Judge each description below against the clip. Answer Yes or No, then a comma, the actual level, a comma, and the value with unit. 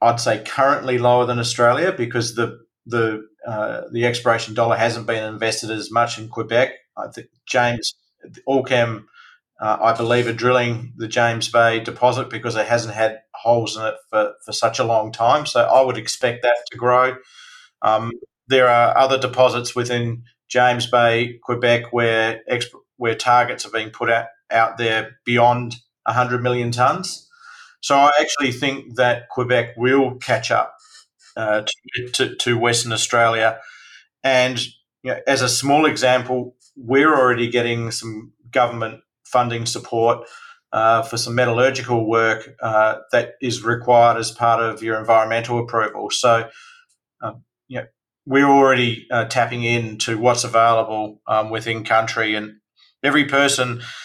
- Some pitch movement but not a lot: No, narrow, 1.6 semitones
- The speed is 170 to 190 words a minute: No, average, 150 wpm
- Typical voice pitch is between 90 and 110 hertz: No, low, 120 Hz